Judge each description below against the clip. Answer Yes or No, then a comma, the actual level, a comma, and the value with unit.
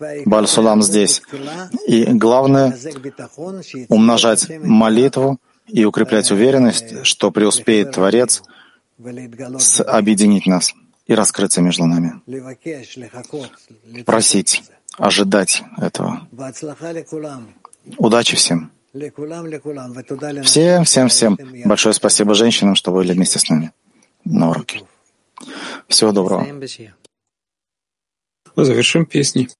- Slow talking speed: Yes, slow, 80 wpm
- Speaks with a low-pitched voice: Yes, low, 120 Hz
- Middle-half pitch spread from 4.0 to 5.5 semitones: Yes, average, 4.9 semitones